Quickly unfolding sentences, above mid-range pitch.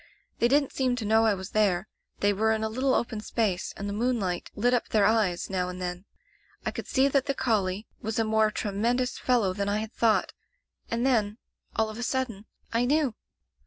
Yes: fast, 225 wpm; high, 220 Hz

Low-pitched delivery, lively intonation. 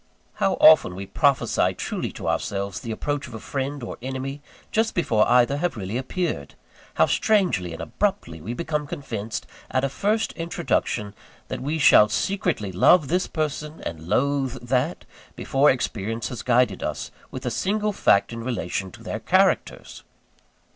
Yes: low, 130 Hz; wide, 6.4 semitones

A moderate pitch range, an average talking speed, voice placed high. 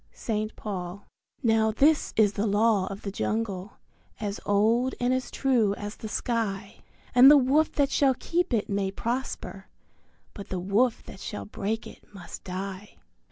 Yes: average, 3.7 semitones; average, 160 wpm; high, 215 Hz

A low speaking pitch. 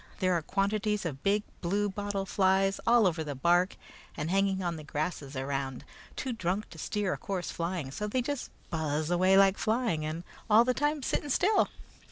No: high, 190 Hz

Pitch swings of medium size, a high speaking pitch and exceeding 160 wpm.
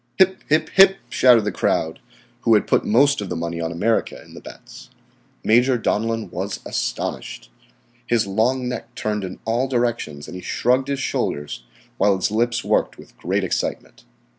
No: average, 4.9 semitones; low, 115 Hz; average, 170 wpm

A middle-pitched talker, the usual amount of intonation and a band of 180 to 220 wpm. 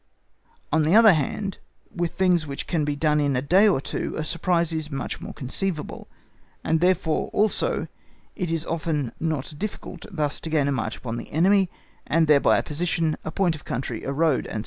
Yes: medium, 160 Hz; average, 3.4 semitones; average, 195 wpm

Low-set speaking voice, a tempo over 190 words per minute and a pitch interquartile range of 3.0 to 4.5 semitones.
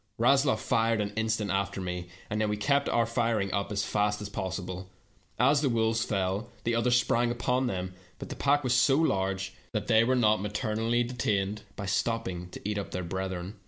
Yes: low, 105 Hz; average, 200 wpm; average, 3.5 semitones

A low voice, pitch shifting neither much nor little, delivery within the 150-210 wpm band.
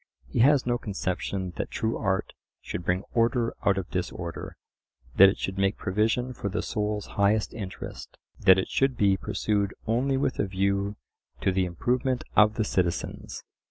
Yes: low, 100 Hz; average, 3.4 semitones; average, 165 wpm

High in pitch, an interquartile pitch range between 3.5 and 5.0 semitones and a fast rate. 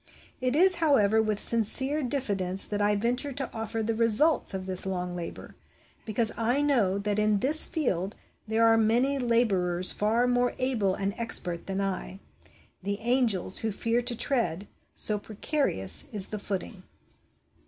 No: high, 220 Hz; average, 3.9 semitones; average, 165 wpm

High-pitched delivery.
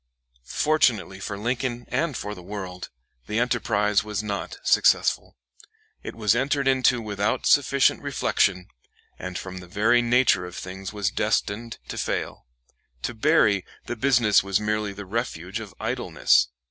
No: low, 105 Hz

